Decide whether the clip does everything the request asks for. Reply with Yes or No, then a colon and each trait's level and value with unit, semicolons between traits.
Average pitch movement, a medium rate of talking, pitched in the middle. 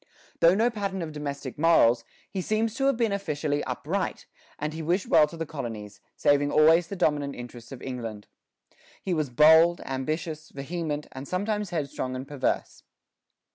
Yes: average, 4.3 semitones; average, 165 wpm; medium, 155 Hz